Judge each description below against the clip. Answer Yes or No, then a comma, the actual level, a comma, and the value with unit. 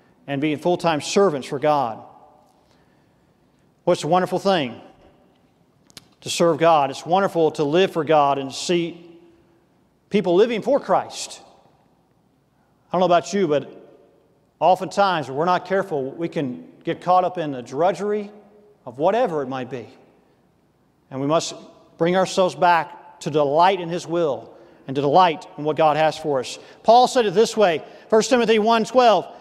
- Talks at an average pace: Yes, average, 160 wpm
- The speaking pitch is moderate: Yes, medium, 170 Hz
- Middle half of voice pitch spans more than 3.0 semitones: Yes, average, 4.0 semitones